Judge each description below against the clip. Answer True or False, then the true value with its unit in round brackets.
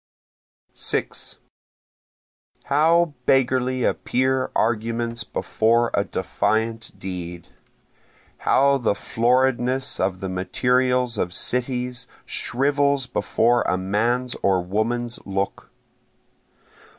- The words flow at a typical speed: False (85 wpm)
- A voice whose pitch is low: True (120 Hz)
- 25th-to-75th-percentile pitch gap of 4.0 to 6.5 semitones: False (3.2 semitones)